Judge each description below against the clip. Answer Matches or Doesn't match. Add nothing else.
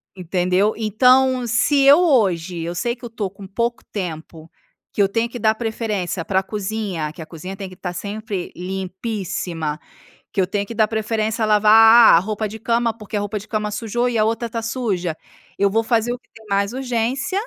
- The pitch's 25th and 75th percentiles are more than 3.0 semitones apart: Matches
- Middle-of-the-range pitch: Doesn't match